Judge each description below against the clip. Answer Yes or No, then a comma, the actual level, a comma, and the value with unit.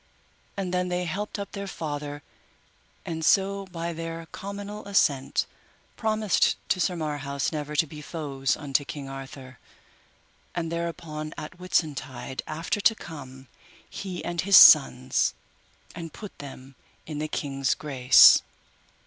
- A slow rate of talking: Yes, slow, 130 wpm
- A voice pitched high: No, medium, 155 Hz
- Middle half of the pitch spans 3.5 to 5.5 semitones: Yes, average, 4.3 semitones